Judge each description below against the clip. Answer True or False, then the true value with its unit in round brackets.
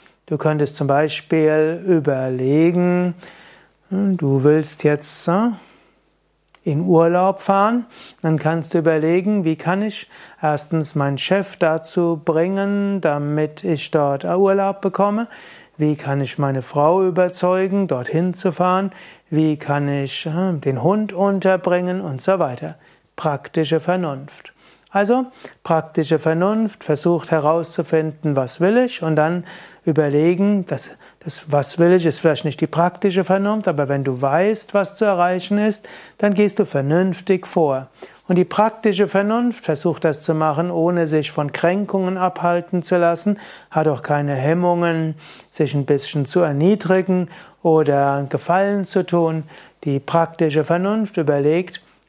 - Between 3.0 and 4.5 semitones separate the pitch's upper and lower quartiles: True (3.7 semitones)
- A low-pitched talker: False (170 Hz)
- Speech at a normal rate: True (135 wpm)